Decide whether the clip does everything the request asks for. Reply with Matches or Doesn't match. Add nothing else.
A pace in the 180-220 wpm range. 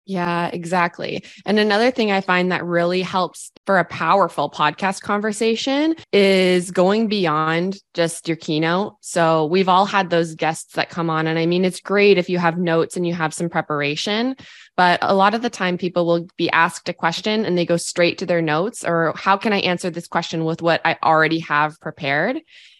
Matches